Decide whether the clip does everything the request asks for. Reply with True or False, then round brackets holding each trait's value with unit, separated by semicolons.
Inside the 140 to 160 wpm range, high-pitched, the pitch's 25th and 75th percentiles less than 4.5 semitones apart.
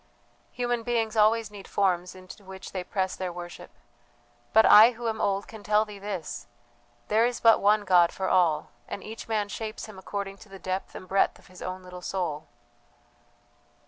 False (185 wpm; 200 Hz; 2.8 semitones)